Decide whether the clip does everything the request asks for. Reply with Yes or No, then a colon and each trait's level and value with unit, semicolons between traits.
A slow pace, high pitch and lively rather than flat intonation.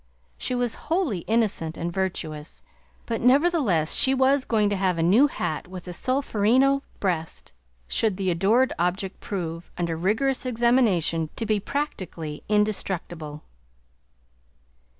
Yes: slow, 130 wpm; high, 200 Hz; wide, 6.6 semitones